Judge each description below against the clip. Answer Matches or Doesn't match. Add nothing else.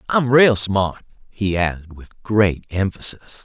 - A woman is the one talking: Doesn't match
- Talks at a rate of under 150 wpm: Matches